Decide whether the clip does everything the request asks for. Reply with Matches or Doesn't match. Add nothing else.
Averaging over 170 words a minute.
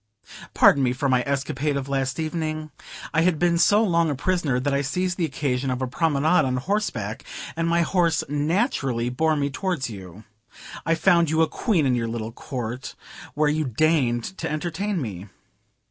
Matches